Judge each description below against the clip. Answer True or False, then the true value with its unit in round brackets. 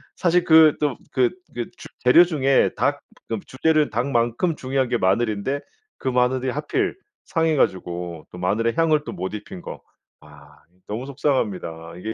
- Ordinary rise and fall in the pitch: False (6.0 semitones)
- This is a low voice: True (125 Hz)